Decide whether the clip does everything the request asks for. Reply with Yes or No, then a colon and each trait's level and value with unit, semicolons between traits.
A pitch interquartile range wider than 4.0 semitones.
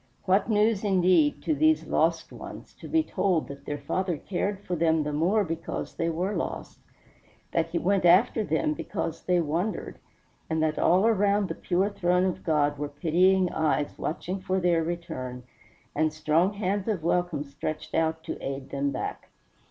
No: average, 3.7 semitones